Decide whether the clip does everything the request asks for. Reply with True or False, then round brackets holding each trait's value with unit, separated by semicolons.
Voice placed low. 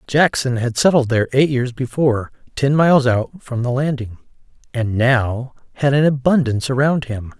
True (130 Hz)